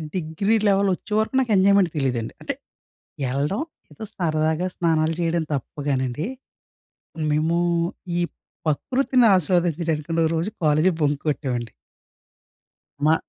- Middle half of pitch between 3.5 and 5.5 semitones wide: Yes, average, 4.4 semitones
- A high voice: No, medium, 165 Hz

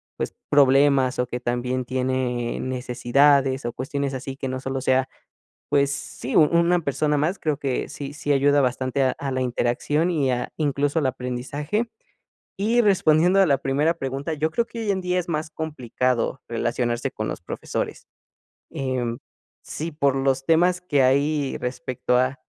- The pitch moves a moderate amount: Yes, average, 3.1 semitones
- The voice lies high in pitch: No, low, 135 Hz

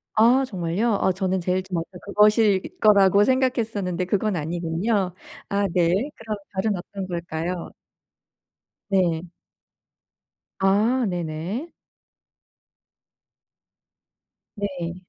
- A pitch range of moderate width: Yes, average, 3.3 semitones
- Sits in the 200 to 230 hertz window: No, high, 190 Hz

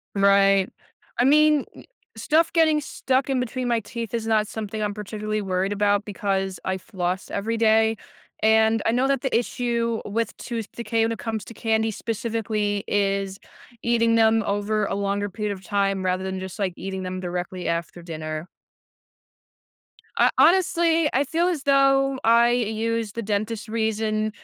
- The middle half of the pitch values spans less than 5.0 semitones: Yes, average, 2.9 semitones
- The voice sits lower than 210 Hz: No, high, 220 Hz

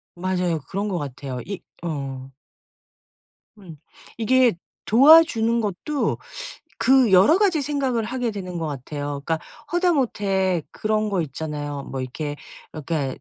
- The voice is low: No, high, 190 Hz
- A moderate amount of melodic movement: No, wide, 7.9 semitones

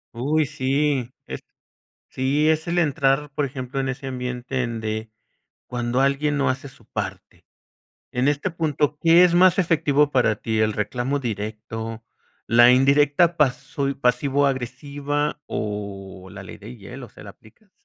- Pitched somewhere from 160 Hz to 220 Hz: No, low, 135 Hz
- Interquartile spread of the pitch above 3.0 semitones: Yes, average, 3.7 semitones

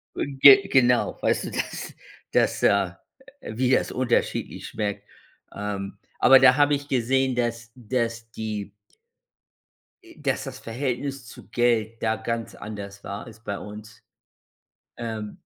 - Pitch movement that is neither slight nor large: Yes, average, 3.4 semitones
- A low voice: Yes, low, 115 Hz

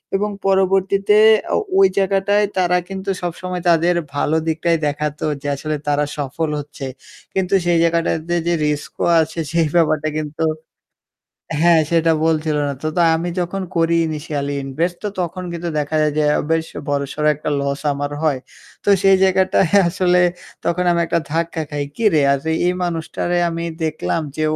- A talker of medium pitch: Yes, medium, 165 Hz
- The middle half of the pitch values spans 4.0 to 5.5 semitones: No, average, 2.9 semitones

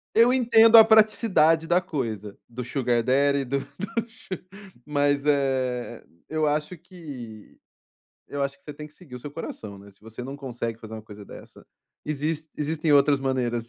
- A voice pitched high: No, medium, 140 Hz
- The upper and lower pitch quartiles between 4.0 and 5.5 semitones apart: Yes, average, 4.8 semitones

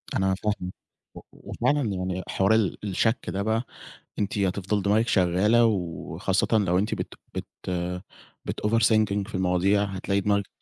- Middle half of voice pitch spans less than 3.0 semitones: Yes, narrow, 2.5 semitones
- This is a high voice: No, low, 100 Hz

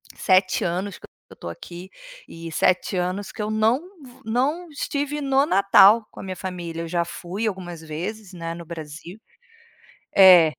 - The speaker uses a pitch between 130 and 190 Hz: Yes, medium, 185 Hz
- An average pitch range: Yes, average, 4.2 semitones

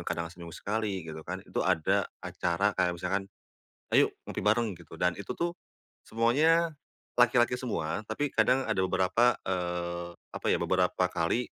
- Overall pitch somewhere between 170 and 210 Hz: No, very low, 95 Hz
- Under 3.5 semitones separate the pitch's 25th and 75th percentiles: No, average, 5.3 semitones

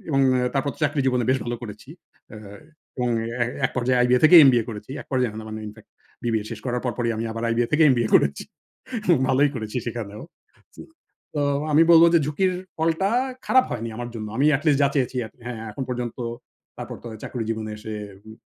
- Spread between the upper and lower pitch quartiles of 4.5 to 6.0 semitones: No, average, 3.7 semitones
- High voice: No, low, 125 Hz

